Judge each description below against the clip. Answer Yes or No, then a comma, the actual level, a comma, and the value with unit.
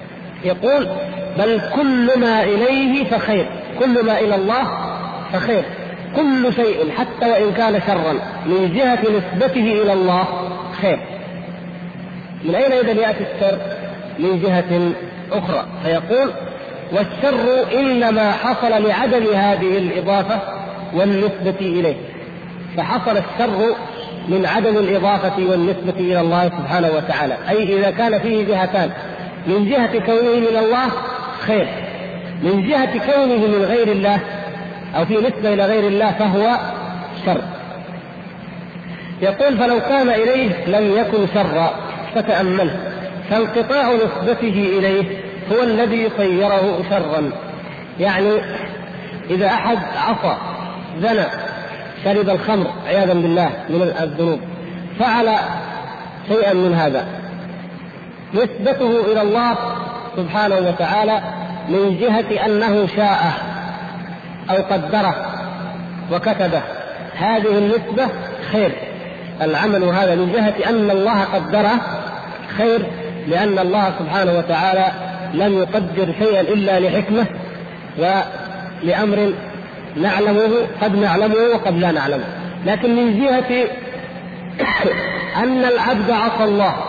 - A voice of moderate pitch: No, high, 200 Hz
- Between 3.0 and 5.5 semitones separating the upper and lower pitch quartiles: Yes, average, 3.4 semitones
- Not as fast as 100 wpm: No, average, 105 wpm